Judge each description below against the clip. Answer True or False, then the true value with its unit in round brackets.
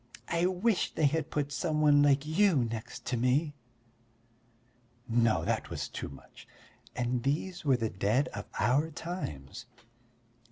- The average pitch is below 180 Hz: True (140 Hz)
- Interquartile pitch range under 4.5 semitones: False (5.1 semitones)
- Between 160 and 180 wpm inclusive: False (145 wpm)